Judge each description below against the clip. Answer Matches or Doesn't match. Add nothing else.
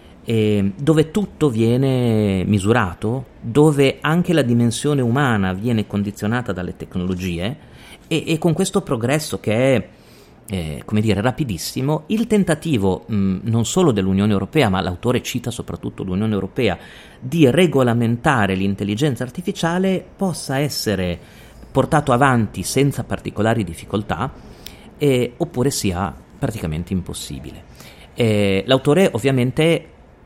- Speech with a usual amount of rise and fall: Doesn't match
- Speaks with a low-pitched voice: Matches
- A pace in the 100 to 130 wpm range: Matches